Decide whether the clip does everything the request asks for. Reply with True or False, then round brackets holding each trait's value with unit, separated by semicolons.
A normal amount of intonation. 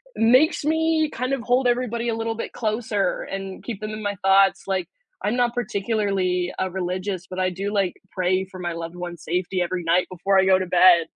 True (3.9 semitones)